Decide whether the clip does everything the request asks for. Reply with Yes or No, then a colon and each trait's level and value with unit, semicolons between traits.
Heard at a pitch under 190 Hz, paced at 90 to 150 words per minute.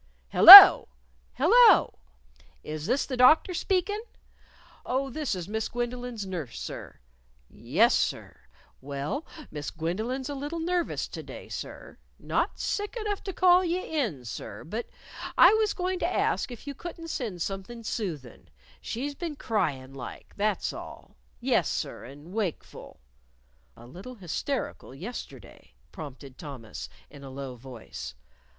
No: high, 220 Hz; average, 140 wpm